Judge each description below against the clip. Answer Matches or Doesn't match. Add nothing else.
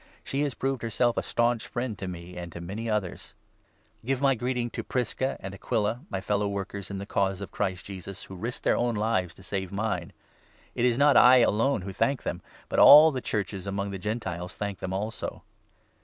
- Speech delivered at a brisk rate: Matches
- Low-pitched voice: Matches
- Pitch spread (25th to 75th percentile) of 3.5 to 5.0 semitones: Matches